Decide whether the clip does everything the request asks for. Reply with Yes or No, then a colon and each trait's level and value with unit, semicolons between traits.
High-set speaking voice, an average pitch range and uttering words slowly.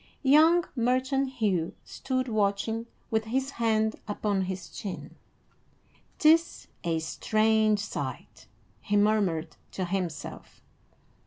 Yes: high, 220 Hz; average, 4.7 semitones; slow, 100 wpm